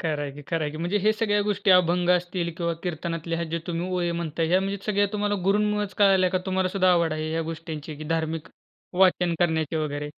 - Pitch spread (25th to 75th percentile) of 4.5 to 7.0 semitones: No, average, 2.8 semitones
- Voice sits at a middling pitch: Yes, medium, 175 Hz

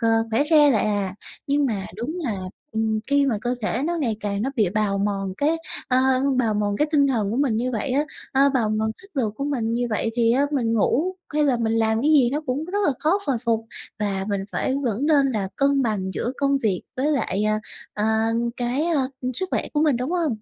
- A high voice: Yes, high, 240 Hz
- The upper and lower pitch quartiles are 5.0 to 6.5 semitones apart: No, average, 4.6 semitones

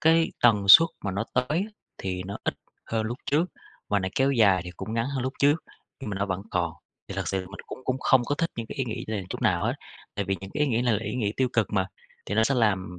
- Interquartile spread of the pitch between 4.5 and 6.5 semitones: Yes, average, 5.2 semitones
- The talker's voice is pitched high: No, low, 110 Hz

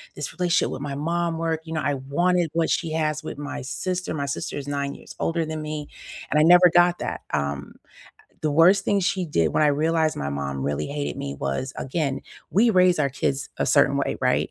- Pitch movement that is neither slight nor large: Yes, average, 3.8 semitones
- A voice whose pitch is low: No, medium, 155 Hz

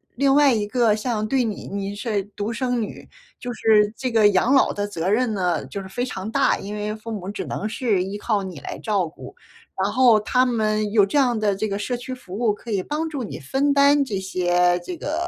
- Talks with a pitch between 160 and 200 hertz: No, high, 215 Hz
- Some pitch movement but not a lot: Yes, average, 3.8 semitones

